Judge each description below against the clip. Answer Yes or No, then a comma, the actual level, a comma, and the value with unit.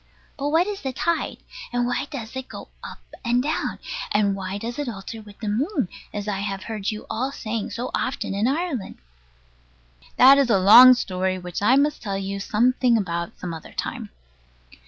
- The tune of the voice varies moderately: Yes, average, 4.9 semitones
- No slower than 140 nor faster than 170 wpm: No, average, 185 wpm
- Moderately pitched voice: No, high, 225 Hz